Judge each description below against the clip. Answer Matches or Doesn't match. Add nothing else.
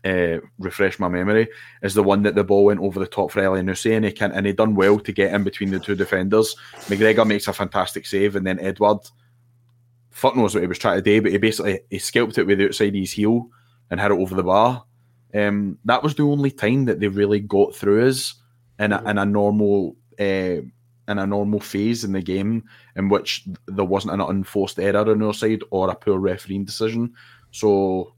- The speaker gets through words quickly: Matches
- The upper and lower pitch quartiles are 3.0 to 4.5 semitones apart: Doesn't match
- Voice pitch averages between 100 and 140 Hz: Matches